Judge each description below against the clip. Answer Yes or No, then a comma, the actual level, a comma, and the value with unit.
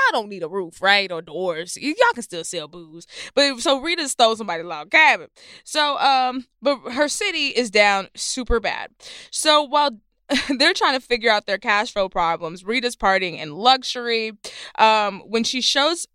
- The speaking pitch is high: Yes, high, 235 Hz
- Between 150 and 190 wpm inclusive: Yes, average, 180 wpm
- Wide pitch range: Yes, wide, 6.4 semitones